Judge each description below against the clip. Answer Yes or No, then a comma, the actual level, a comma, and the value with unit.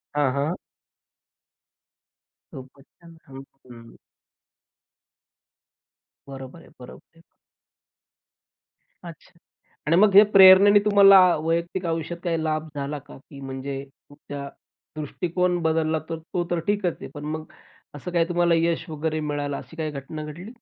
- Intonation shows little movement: No, average, 3.3 semitones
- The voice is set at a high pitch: No, medium, 160 Hz